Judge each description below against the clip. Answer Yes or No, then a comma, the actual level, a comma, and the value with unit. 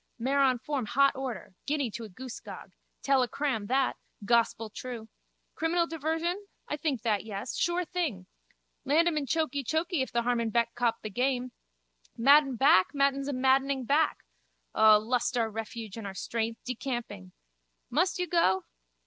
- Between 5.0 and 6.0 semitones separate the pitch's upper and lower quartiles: No, average, 4.1 semitones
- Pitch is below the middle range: No, very high, 255 Hz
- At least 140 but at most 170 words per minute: Yes, average, 155 wpm